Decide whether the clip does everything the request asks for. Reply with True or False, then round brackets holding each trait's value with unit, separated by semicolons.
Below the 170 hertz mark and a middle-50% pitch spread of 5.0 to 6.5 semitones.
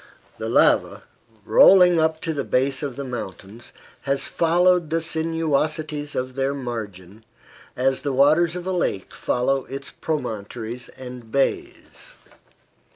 False (140 Hz; 4.4 semitones)